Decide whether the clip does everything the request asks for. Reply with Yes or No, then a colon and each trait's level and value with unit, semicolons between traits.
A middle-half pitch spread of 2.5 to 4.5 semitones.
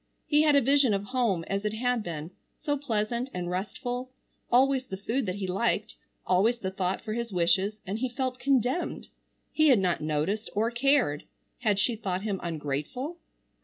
No: average, 5.2 semitones